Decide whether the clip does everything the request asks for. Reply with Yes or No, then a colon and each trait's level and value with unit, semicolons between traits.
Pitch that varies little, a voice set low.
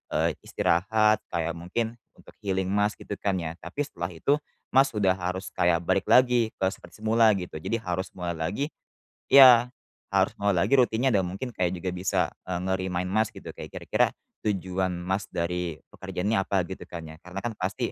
No: average, 3.7 semitones; very low, 95 Hz